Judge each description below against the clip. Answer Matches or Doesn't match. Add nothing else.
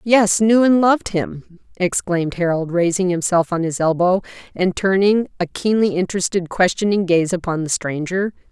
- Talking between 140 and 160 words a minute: Matches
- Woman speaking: Matches